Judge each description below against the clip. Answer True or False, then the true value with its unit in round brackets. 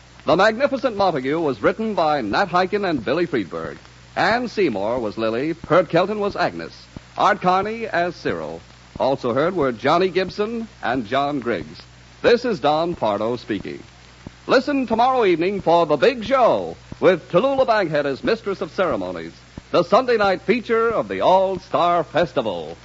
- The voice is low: False (180 Hz)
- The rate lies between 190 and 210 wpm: False (155 wpm)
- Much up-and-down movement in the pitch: True (7.2 semitones)